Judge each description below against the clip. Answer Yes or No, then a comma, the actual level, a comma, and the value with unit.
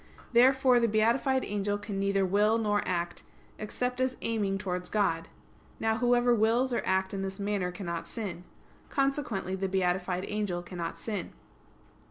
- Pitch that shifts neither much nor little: Yes, average, 3.6 semitones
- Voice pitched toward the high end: Yes, high, 205 Hz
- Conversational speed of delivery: Yes, average, 150 wpm